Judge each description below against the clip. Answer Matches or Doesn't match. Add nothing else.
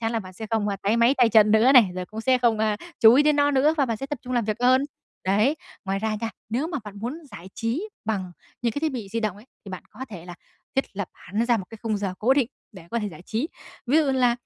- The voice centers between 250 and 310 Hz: Doesn't match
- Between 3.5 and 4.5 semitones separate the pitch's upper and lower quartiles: Matches